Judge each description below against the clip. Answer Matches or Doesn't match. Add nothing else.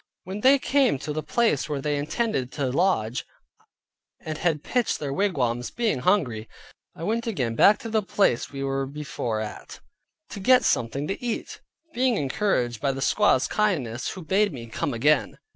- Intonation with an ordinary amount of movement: Doesn't match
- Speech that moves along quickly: Doesn't match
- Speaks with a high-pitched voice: Doesn't match